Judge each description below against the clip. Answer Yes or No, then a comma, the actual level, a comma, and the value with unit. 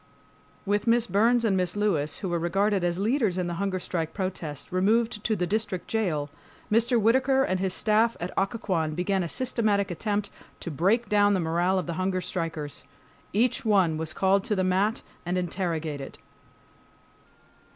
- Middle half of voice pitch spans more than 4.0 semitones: No, average, 3.6 semitones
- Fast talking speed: No, average, 170 wpm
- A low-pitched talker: No, high, 190 Hz